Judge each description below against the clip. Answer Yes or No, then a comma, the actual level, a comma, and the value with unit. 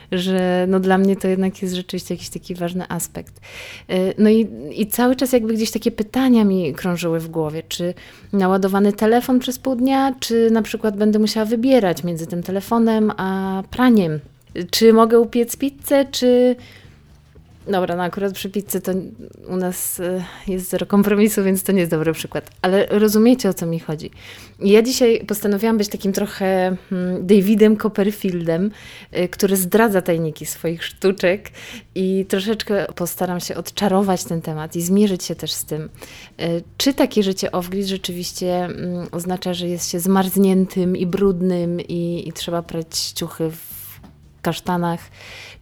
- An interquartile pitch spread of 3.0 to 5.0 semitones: Yes, average, 3.6 semitones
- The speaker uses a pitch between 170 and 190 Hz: Yes, medium, 185 Hz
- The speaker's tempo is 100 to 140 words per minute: No, average, 150 wpm